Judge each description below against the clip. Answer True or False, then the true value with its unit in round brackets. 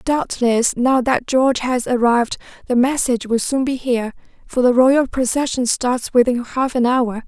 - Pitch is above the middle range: True (250 Hz)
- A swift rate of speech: False (175 wpm)